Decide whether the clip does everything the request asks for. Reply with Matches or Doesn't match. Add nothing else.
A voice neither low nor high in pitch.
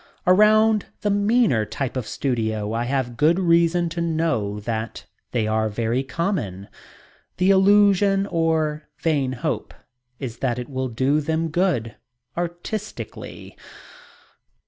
Matches